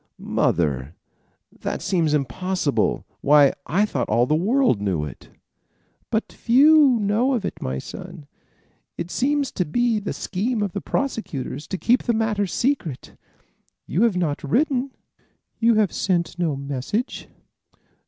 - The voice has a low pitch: No, high, 195 Hz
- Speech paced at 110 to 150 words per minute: Yes, average, 140 wpm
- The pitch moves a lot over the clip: Yes, wide, 8.6 semitones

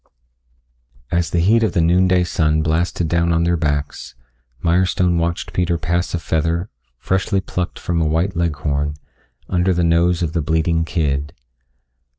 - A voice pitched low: Yes, very low, 85 Hz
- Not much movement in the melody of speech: Yes, narrow, 1.7 semitones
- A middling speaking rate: Yes, average, 160 wpm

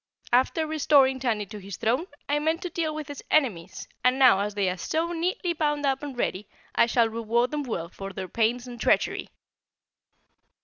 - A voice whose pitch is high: Yes, very high, 255 Hz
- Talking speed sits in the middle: Yes, average, 190 wpm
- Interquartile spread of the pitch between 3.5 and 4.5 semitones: No, wide, 5.6 semitones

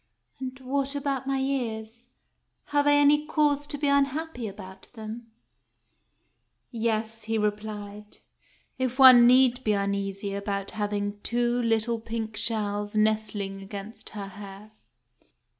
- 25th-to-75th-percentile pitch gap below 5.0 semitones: Yes, average, 4.0 semitones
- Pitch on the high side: Yes, high, 225 Hz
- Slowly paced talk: Yes, slow, 130 wpm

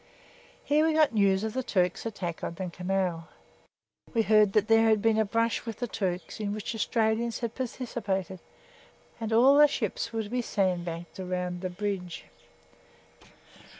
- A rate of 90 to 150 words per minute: No, average, 165 wpm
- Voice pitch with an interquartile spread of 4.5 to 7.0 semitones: No, average, 3.7 semitones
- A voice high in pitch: Yes, high, 210 Hz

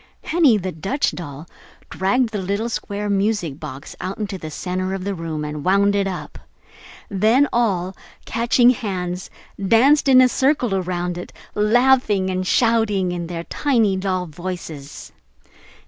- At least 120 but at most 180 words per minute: Yes, average, 145 wpm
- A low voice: No, high, 195 Hz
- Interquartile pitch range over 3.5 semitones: Yes, average, 4.1 semitones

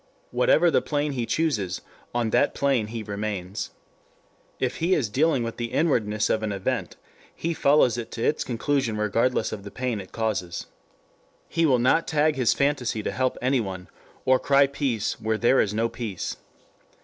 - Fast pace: No, average, 175 wpm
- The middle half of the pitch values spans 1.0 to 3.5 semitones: No, average, 4.5 semitones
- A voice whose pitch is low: Yes, low, 120 Hz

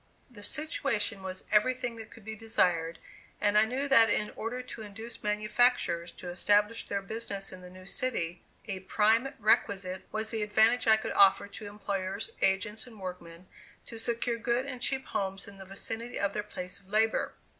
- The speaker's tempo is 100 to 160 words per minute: No, average, 180 wpm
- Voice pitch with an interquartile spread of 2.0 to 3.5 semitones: Yes, average, 3.0 semitones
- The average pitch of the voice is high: Yes, high, 210 Hz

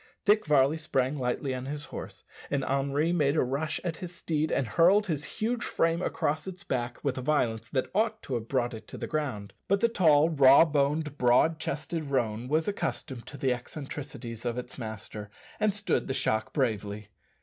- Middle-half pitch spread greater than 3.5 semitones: Yes, average, 4.4 semitones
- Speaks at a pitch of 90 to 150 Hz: Yes, medium, 140 Hz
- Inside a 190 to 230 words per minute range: Yes, average, 195 wpm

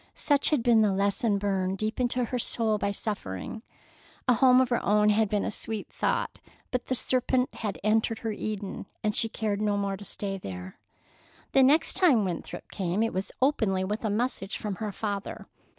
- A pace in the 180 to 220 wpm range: Yes, average, 195 wpm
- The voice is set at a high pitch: Yes, high, 215 Hz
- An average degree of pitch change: Yes, average, 3.1 semitones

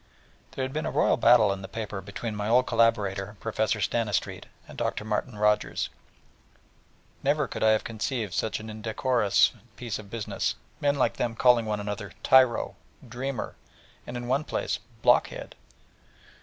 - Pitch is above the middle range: No, low, 110 Hz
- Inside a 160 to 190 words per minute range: Yes, average, 165 wpm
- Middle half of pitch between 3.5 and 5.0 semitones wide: No, average, 2.8 semitones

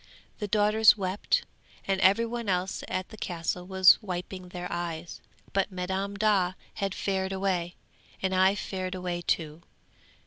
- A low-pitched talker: No, high, 190 Hz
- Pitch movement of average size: No, narrow, 1.7 semitones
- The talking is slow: No, average, 145 wpm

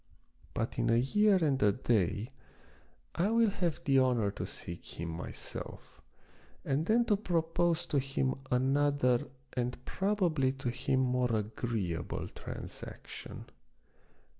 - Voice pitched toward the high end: No, low, 135 Hz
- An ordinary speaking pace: No, slow, 125 wpm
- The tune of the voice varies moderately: No, wide, 5.9 semitones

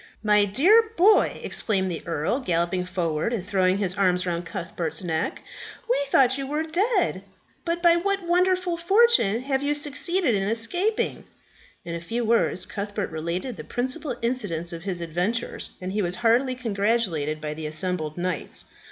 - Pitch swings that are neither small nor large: No, wide, 8.3 semitones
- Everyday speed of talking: Yes, average, 160 wpm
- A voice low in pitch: No, high, 210 Hz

